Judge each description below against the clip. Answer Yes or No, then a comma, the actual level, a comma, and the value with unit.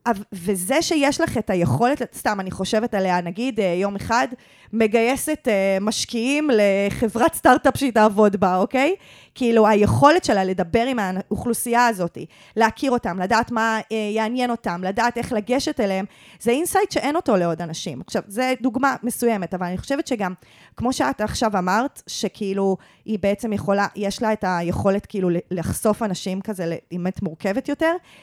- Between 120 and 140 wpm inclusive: No, fast, 150 wpm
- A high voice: Yes, high, 220 Hz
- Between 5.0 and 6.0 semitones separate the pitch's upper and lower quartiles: No, average, 4.4 semitones